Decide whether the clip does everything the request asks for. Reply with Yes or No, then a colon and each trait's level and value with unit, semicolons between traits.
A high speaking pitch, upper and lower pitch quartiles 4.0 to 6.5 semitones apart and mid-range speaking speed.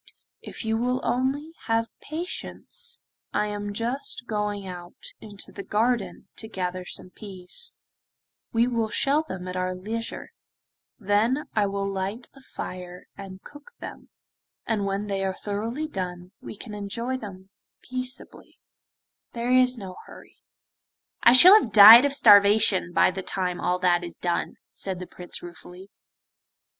Yes: high, 205 Hz; average, 4.5 semitones; average, 150 wpm